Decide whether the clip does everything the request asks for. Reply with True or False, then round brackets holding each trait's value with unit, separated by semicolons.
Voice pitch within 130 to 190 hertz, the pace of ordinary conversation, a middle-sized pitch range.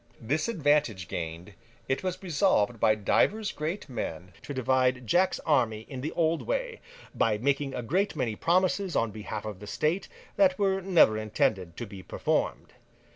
False (135 Hz; 165 wpm; 8.8 semitones)